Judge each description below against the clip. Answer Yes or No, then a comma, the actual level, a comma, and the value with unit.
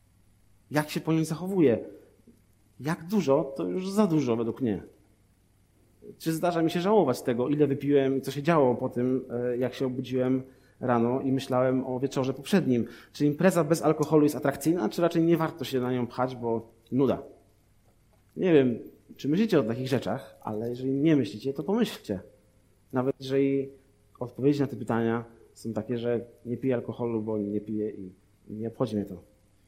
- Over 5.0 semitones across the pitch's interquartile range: No, average, 4.5 semitones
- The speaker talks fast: Yes, fast, 170 wpm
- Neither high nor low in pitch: No, low, 125 Hz